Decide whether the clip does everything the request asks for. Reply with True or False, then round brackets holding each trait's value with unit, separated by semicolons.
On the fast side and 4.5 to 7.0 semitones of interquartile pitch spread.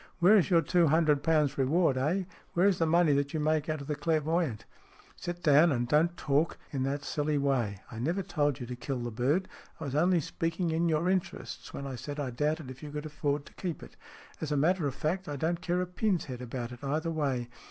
False (245 wpm; 3.5 semitones)